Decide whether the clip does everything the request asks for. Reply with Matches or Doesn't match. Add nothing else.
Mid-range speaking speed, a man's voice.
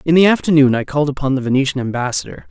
Doesn't match